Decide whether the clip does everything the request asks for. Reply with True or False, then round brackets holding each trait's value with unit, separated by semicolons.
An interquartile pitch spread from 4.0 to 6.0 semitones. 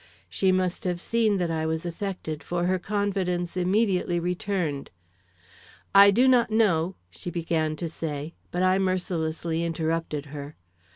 False (3.1 semitones)